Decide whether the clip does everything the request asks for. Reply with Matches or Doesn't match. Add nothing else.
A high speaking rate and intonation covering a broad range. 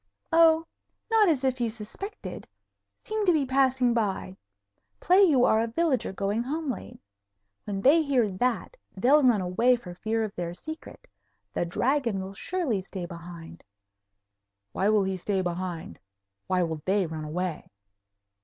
Doesn't match